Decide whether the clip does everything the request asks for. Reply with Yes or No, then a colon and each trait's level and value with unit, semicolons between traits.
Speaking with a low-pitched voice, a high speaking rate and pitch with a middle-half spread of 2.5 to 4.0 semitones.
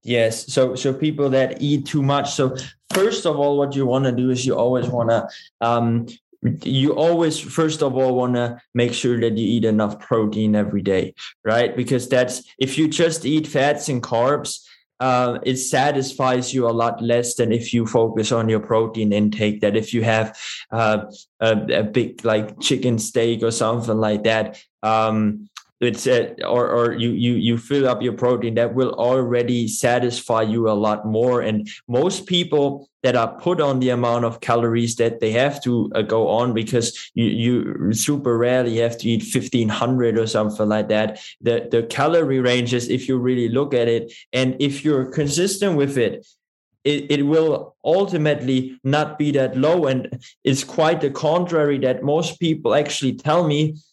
No: low, 125 Hz; average, 185 wpm; average, 3.4 semitones